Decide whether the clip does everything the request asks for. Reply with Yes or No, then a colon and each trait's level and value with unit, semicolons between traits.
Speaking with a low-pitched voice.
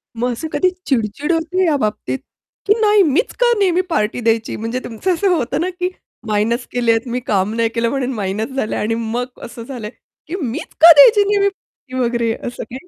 No: very high, 250 Hz